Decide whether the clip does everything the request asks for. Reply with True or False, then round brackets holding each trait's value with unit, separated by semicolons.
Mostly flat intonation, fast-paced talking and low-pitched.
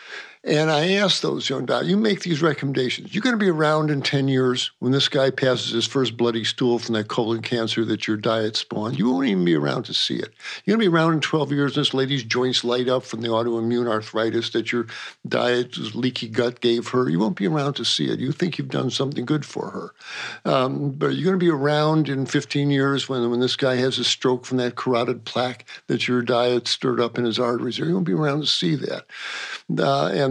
False (3.5 semitones; 240 wpm; 130 Hz)